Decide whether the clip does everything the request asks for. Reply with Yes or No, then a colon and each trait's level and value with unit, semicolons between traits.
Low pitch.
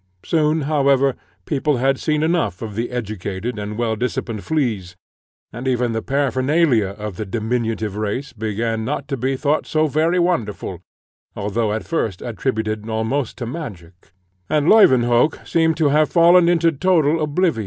Yes: low, 125 Hz